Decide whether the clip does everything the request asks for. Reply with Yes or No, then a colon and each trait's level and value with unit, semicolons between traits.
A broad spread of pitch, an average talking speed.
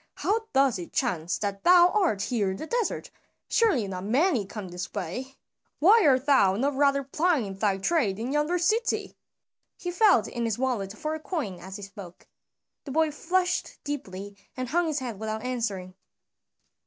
Yes: wide, 8.0 semitones; average, 175 wpm